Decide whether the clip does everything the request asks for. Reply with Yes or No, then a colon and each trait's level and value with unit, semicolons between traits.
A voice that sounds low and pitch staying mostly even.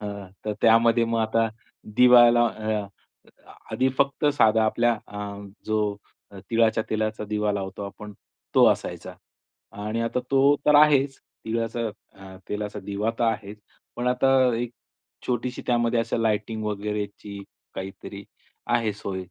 Yes: low, 110 Hz; narrow, 2.3 semitones